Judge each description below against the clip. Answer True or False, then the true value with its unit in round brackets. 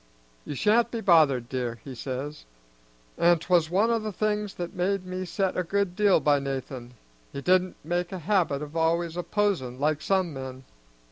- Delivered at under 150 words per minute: False (185 wpm)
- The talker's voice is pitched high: False (175 Hz)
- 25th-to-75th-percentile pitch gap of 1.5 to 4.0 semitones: False (5.4 semitones)